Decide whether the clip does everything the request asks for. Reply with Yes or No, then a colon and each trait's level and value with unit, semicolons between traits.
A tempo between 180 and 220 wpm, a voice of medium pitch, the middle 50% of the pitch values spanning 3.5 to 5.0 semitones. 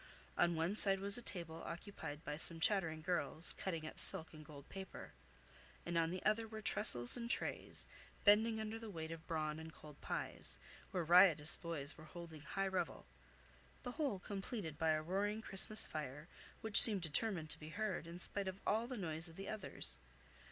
Yes: average, 185 wpm; medium, 175 Hz; average, 4.5 semitones